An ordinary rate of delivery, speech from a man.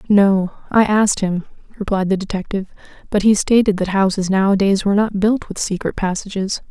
No: average, 170 wpm; female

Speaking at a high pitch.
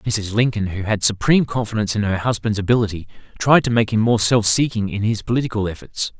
No: low, 110 Hz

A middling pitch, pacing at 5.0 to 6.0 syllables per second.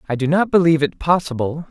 No: medium, 155 Hz; 6.5 syllables/s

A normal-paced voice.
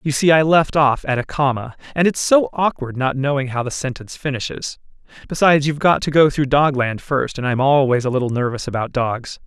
No: fast, 215 wpm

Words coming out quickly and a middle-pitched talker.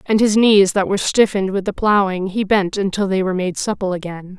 No: fast, 235 wpm; high, 195 Hz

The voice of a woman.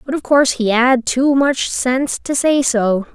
Yes: female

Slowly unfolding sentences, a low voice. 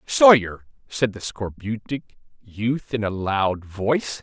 Yes: slow, 130 wpm; low, 110 Hz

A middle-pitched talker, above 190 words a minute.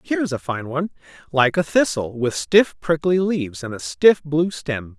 Yes: medium, 150 Hz; fast, 205 wpm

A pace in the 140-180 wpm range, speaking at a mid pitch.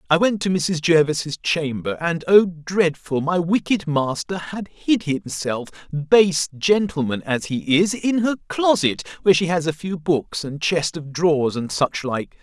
Yes: average, 175 wpm; medium, 165 Hz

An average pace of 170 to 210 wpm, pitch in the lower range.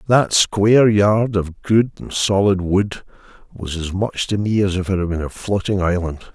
Yes: average, 200 wpm; low, 100 Hz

